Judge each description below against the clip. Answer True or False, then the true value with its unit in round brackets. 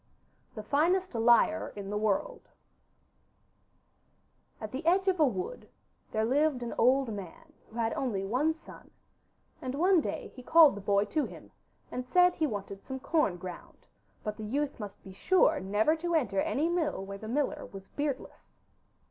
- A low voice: False (255 Hz)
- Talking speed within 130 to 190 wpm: True (170 wpm)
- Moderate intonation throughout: False (7.2 semitones)